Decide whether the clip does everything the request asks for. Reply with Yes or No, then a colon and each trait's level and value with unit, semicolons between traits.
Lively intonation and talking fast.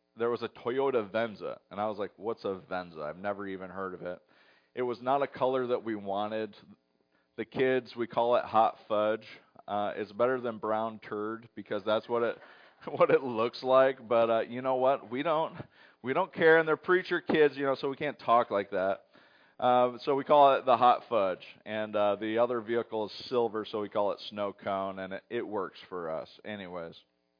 No: average, 3.9 semitones; fast, 210 wpm